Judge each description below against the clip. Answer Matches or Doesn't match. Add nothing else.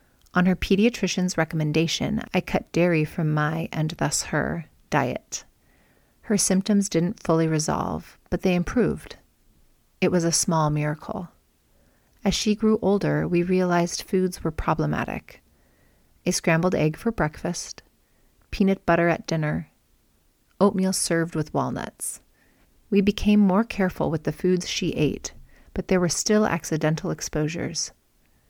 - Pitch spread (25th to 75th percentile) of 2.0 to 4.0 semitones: Matches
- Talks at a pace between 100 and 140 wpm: Matches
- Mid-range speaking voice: Matches